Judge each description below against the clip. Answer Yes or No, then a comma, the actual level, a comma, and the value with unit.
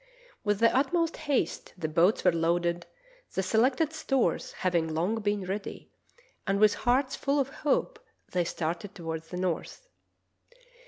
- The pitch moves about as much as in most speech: No, wide, 7.4 semitones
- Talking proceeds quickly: No, average, 145 wpm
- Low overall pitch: No, high, 205 Hz